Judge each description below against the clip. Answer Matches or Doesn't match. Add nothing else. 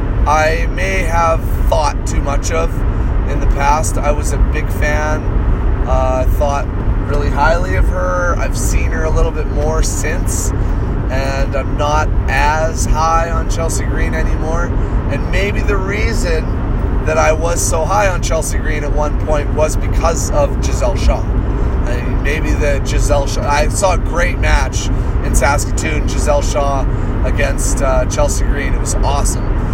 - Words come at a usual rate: Matches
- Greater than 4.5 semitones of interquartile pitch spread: Doesn't match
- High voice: Doesn't match